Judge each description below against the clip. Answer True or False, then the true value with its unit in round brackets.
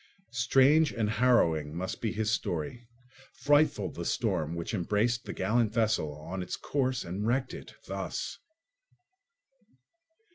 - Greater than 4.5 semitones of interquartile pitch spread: True (5.6 semitones)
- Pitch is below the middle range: True (110 Hz)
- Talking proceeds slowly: True (120 wpm)